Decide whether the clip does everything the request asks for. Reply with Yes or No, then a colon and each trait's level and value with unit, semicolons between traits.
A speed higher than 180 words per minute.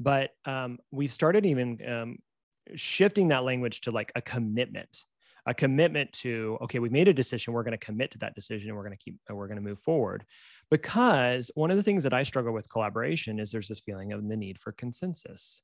Yes: fast, 205 wpm